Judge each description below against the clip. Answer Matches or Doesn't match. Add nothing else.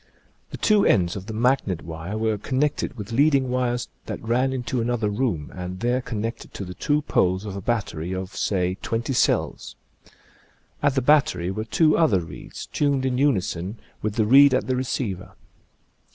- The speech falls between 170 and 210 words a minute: Matches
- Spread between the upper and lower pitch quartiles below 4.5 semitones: Doesn't match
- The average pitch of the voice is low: Matches